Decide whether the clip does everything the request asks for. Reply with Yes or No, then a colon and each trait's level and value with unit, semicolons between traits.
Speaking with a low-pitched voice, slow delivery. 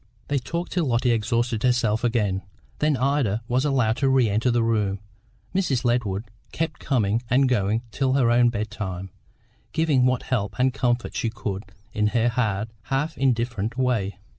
No: low, 120 Hz; average, 165 wpm